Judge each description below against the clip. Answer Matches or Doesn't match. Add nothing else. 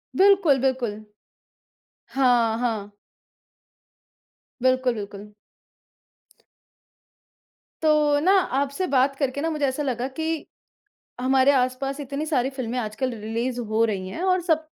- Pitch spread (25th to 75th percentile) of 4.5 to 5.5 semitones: Doesn't match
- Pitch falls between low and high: Doesn't match